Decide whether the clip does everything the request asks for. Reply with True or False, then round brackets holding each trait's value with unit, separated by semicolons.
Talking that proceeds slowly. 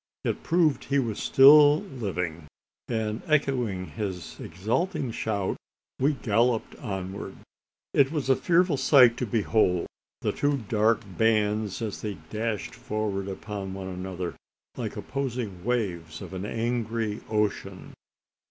True (125 wpm)